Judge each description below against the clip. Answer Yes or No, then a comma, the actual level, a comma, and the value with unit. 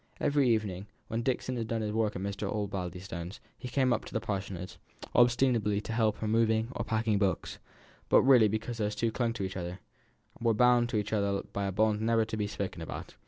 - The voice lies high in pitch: No, low, 110 Hz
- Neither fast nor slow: No, fast, 215 wpm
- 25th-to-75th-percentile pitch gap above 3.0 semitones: No, narrow, 2.6 semitones